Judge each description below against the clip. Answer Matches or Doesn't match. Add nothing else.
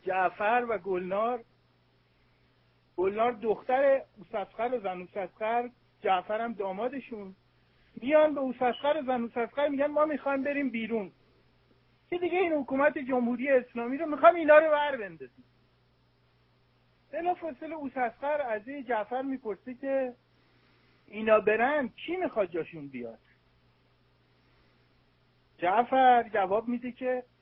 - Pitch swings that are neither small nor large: Doesn't match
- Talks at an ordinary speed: Doesn't match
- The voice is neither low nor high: Doesn't match